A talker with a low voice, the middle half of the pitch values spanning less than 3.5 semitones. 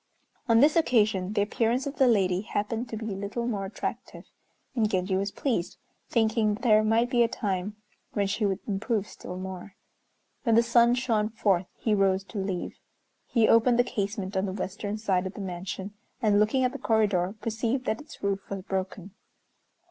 No: high, 210 Hz; average, 3.0 semitones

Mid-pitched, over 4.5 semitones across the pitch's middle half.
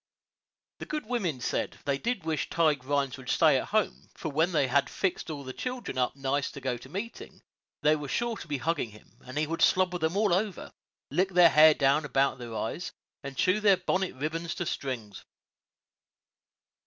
Yes: medium, 155 Hz; average, 5.2 semitones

